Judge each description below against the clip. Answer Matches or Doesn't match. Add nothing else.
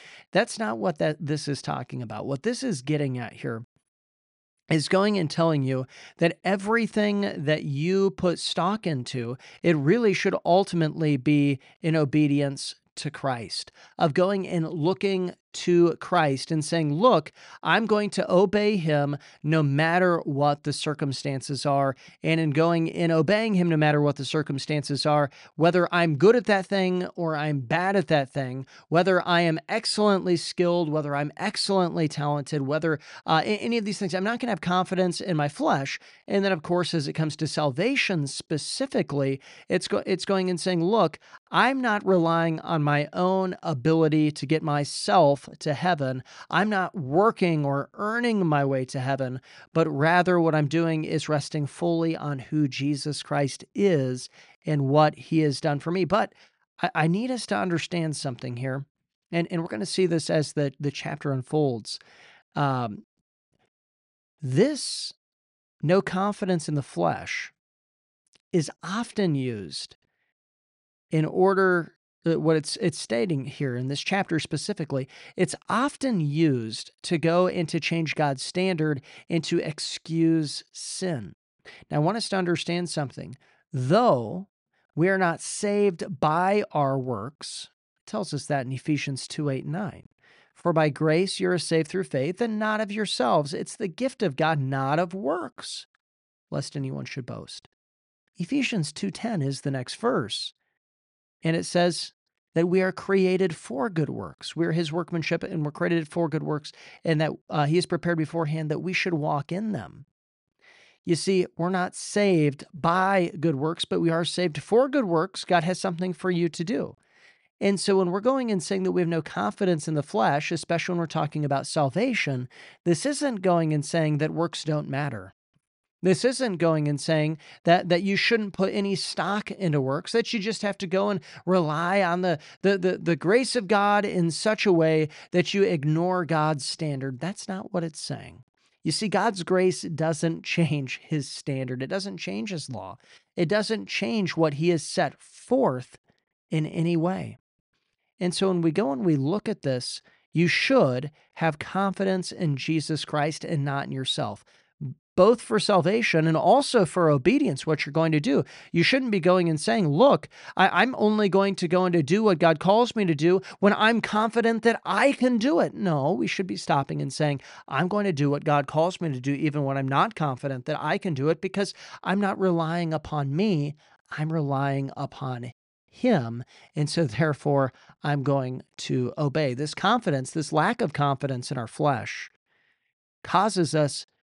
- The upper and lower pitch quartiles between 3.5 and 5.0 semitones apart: Matches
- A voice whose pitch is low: Doesn't match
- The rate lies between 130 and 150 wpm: Doesn't match